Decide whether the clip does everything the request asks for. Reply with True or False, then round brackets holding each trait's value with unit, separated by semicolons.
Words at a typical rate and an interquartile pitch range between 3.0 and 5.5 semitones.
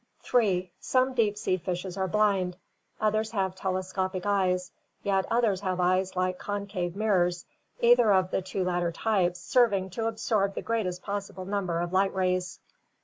False (155 wpm; 2.4 semitones)